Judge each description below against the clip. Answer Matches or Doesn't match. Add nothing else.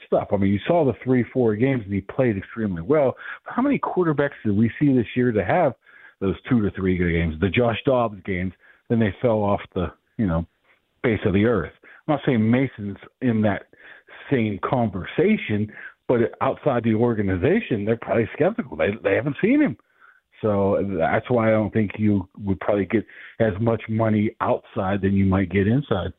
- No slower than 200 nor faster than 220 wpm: Doesn't match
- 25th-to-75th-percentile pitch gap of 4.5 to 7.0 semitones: Doesn't match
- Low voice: Matches